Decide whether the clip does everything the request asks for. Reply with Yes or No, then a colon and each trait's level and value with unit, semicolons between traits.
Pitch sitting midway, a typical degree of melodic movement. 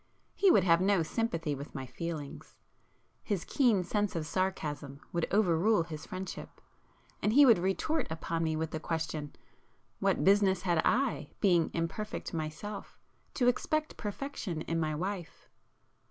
Yes: medium, 175 Hz; average, 4.5 semitones